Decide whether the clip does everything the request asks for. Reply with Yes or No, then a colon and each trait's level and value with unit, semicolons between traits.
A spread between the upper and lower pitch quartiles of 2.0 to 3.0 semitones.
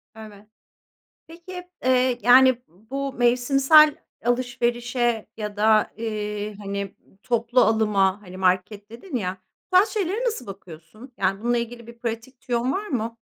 No: average, 3.6 semitones